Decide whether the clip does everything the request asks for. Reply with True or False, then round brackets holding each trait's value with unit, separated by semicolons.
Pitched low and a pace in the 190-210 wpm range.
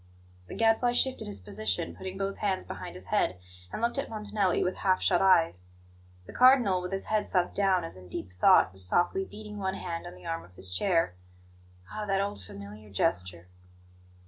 False (180 Hz; 195 wpm)